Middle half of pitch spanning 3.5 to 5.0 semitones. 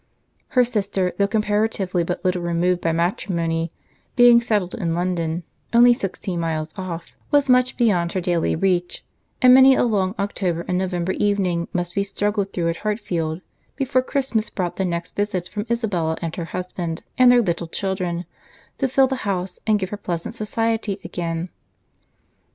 Yes: average, 4.0 semitones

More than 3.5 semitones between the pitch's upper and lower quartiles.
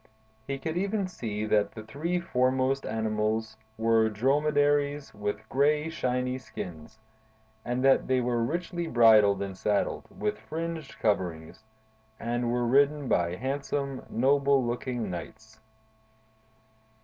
Yes: average, 4.5 semitones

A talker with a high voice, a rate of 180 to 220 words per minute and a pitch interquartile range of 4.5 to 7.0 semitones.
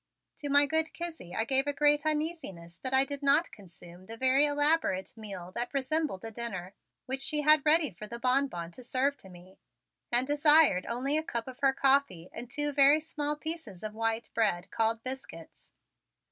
Yes: very high, 265 Hz; average, 190 wpm; average, 5.2 semitones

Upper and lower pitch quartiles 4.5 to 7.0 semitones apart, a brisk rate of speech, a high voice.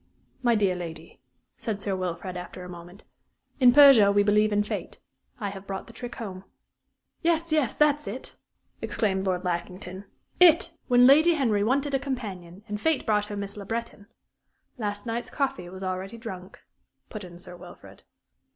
No: average, 4.9 semitones; average, 170 wpm; high, 205 Hz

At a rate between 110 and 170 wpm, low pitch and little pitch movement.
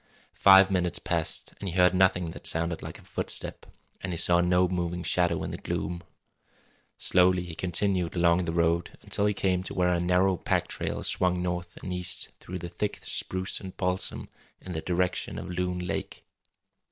No: average, 185 wpm; very low, 90 Hz; narrow, 1.0 semitones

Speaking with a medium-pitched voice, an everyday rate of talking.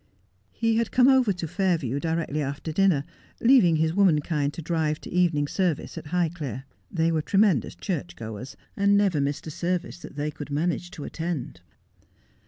Yes: medium, 165 Hz; average, 170 wpm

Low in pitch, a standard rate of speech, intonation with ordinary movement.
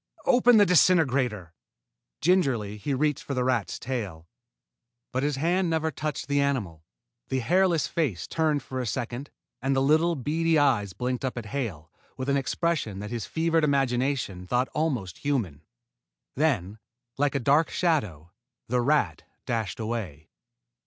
No: low, 130 Hz; average, 150 wpm; wide, 5.7 semitones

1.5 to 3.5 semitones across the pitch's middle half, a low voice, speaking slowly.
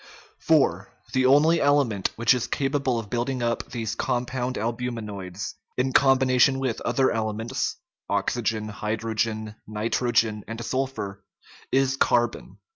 Yes: average, 3.2 semitones; low, 120 Hz; slow, 120 wpm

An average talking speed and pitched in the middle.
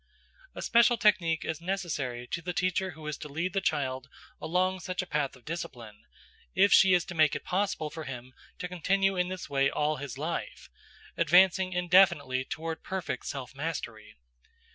Yes: average, 175 wpm; medium, 165 Hz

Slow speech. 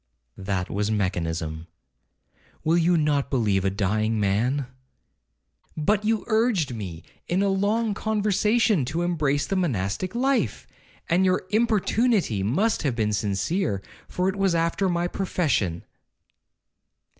Yes: slow, 120 wpm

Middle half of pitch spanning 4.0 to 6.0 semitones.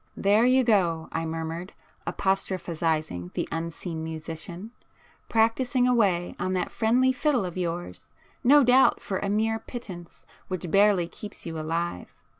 Yes: average, 5.2 semitones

